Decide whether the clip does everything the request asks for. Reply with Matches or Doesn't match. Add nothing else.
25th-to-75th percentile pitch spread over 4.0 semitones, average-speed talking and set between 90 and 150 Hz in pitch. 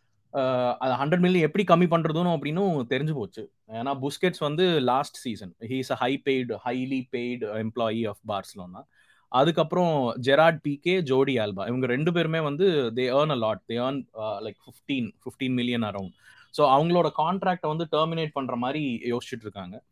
Doesn't match